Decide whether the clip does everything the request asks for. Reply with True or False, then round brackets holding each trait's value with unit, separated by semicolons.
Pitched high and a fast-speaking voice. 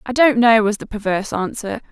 True (220 Hz; 220 wpm)